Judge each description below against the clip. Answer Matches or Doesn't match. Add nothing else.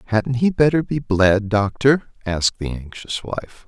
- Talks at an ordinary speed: Matches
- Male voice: Matches